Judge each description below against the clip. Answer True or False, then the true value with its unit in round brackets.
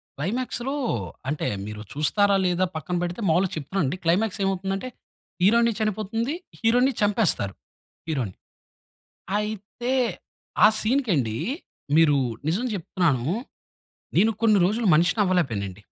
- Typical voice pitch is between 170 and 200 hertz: True (190 Hz)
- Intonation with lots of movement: True (5.8 semitones)